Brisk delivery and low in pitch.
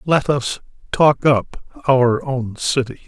No: slow, 135 wpm; low, 130 Hz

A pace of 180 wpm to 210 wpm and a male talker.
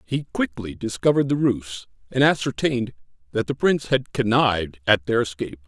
No: average, 160 wpm; male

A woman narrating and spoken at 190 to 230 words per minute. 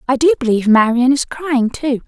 Yes: female; average, 200 wpm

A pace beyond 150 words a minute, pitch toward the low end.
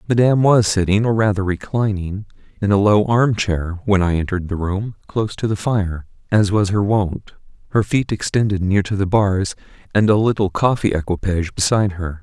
Yes: average, 185 wpm; low, 100 Hz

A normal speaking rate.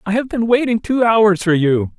No: fast, 240 wpm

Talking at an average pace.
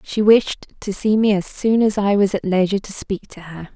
No: fast, 255 wpm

